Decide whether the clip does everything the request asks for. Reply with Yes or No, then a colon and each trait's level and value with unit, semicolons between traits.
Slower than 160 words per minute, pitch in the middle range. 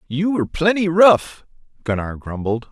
Yes: slow, 135 wpm; medium, 150 Hz